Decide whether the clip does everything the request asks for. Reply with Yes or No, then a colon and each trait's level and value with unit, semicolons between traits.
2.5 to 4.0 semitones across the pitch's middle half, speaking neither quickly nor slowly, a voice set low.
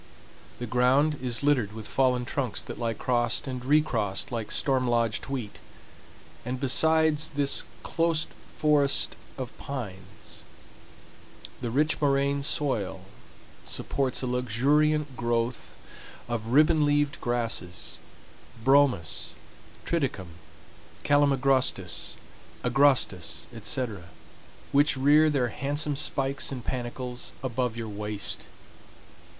No: average, 3.4 semitones; slow, 100 wpm; low, 130 Hz